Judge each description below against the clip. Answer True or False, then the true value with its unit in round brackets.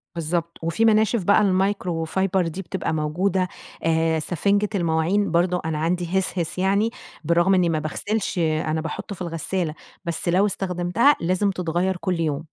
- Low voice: False (175 Hz)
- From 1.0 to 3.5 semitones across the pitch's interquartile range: True (2.9 semitones)